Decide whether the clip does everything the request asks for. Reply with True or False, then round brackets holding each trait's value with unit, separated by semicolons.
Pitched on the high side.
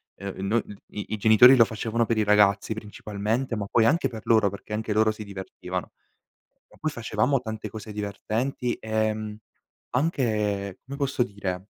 False (110 Hz)